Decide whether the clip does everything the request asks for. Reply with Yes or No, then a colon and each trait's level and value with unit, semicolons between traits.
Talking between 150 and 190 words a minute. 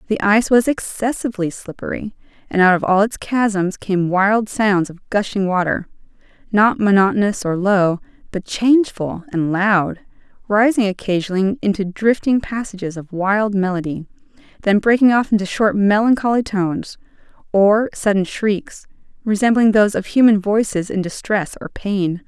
No: average, 140 wpm